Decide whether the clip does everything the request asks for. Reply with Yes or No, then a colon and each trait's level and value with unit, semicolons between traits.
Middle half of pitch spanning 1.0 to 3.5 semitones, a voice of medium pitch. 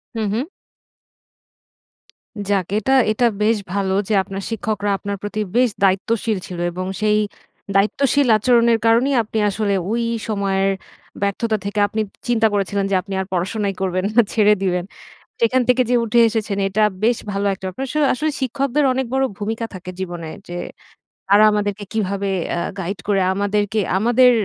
No: average, 2.8 semitones; high, 210 Hz